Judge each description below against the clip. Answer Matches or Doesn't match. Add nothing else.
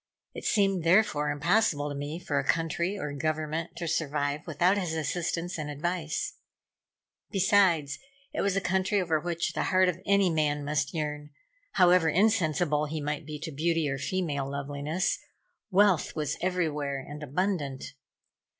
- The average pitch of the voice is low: Doesn't match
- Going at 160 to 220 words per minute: Doesn't match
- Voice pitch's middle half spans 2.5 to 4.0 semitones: Matches